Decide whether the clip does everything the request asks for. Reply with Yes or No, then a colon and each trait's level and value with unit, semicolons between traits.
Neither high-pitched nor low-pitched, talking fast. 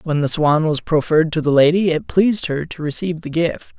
Yes: medium, 160 Hz; fast, 240 wpm